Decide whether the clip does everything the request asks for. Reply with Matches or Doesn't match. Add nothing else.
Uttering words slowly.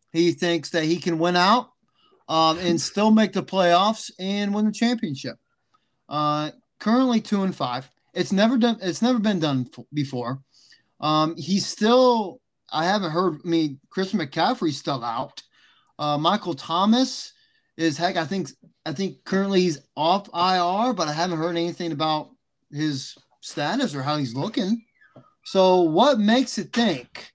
Doesn't match